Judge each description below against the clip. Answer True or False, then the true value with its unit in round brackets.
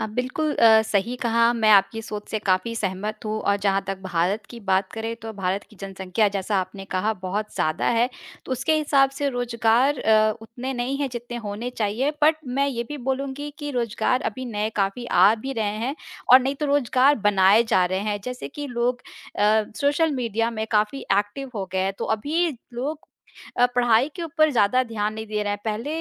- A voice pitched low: False (225 Hz)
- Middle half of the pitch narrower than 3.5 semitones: False (3.8 semitones)